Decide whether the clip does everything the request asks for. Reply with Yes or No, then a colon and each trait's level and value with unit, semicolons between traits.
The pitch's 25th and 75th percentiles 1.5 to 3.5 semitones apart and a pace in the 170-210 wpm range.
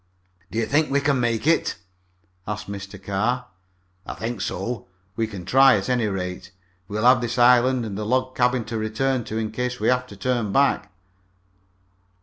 Yes: average, 3.2 semitones; average, 180 wpm